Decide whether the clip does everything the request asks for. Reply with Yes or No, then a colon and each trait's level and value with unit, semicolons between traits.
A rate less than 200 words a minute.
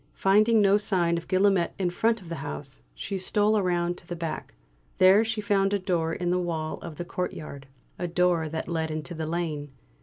No: fast, 205 wpm